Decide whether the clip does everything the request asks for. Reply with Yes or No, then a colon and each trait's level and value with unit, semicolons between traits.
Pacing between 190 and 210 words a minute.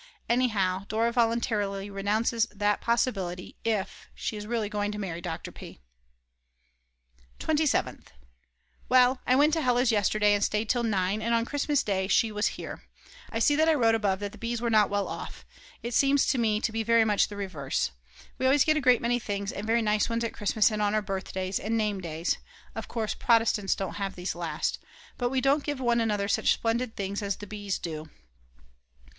Yes: average, 195 wpm